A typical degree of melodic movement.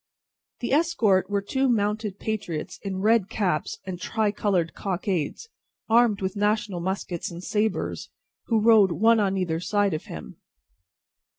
Yes: average, 3.0 semitones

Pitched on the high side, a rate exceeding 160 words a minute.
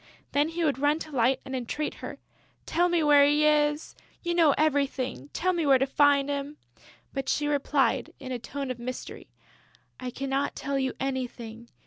Yes: very high, 280 Hz; average, 180 wpm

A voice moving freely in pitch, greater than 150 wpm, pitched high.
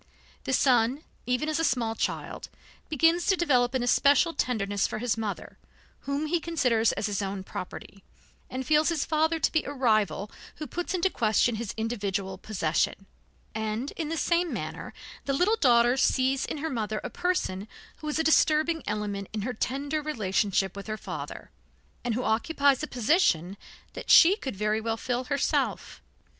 Yes: wide, 6.1 semitones; average, 175 wpm; very high, 250 Hz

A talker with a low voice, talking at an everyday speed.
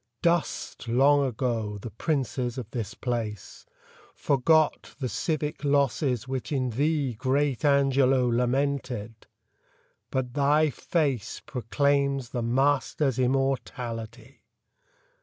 No: low, 130 Hz; slow, 100 wpm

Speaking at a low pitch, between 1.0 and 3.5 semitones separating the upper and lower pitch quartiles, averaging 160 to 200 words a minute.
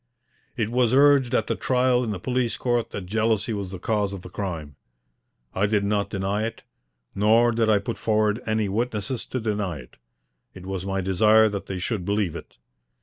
Yes: low, 105 Hz; average, 3.0 semitones; average, 195 wpm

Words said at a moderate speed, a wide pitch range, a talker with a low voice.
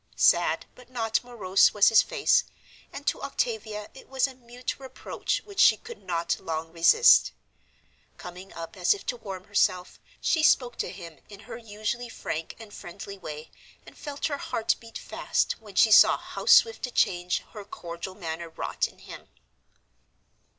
No: average, 170 wpm; wide, 5.7 semitones; high, 210 Hz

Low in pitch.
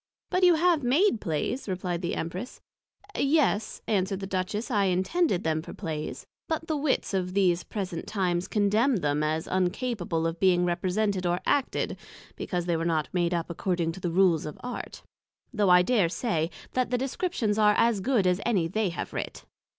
No: high, 190 Hz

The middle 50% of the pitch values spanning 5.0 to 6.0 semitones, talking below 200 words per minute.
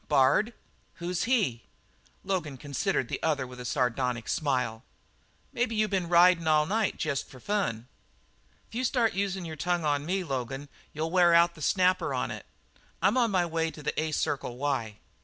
Yes: wide, 5.6 semitones; average, 175 wpm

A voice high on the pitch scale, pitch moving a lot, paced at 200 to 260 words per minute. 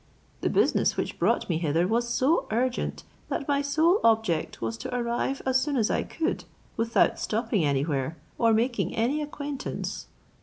No: high, 235 Hz; wide, 6.3 semitones; average, 160 wpm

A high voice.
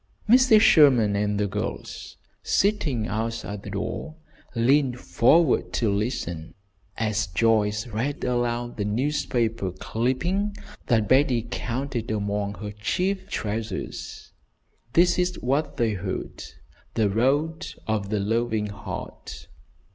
No: low, 115 Hz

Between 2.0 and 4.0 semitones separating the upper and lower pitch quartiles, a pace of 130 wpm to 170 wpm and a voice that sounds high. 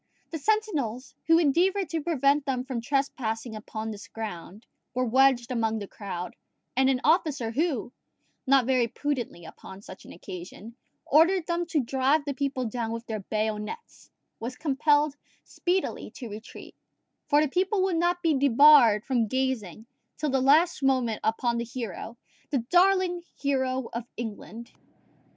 No: average, 5.0 semitones; average, 150 wpm; very high, 260 Hz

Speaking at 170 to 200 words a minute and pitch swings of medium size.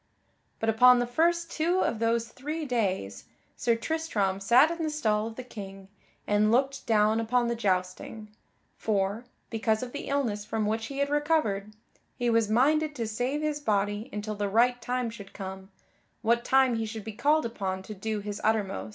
Yes: average, 185 wpm; average, 3.8 semitones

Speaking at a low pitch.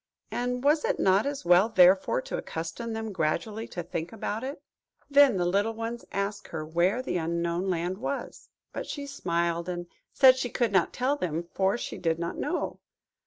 No: high, 195 Hz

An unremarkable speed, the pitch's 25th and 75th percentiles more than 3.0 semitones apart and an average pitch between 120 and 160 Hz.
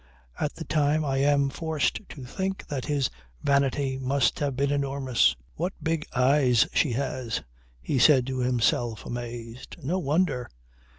No: average, 150 wpm; average, 2.7 semitones; low, 135 Hz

